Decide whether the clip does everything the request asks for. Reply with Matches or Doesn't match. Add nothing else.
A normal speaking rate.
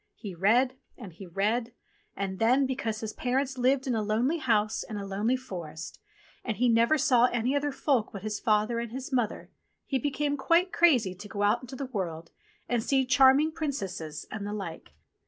Matches